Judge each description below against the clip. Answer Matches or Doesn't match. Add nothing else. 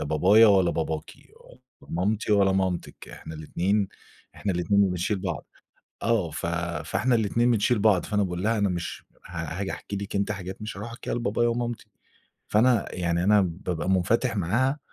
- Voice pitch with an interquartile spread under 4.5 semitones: Matches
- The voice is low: Matches